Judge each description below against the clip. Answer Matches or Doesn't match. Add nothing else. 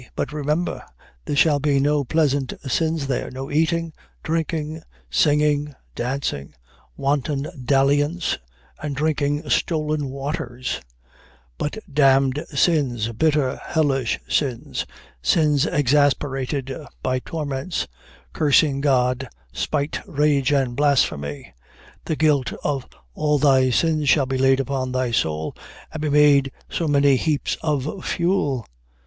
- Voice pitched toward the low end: Doesn't match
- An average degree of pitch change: Doesn't match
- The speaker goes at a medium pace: Doesn't match